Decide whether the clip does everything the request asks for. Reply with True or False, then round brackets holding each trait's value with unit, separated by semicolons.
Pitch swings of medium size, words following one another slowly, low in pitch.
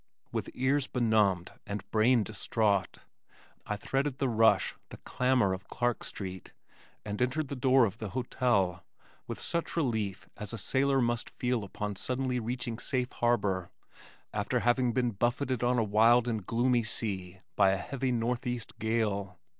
False (3.6 semitones; 155 wpm; 115 Hz)